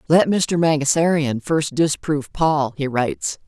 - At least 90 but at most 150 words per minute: Yes, average, 140 wpm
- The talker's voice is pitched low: No, medium, 150 Hz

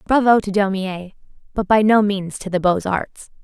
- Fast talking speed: No, average, 190 wpm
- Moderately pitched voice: No, high, 200 Hz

